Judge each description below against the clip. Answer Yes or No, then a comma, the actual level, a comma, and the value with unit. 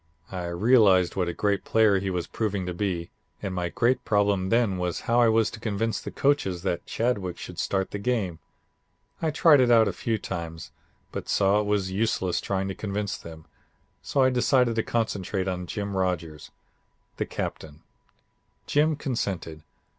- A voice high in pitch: No, low, 100 Hz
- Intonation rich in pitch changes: No, average, 4.0 semitones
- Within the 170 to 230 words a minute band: Yes, average, 175 wpm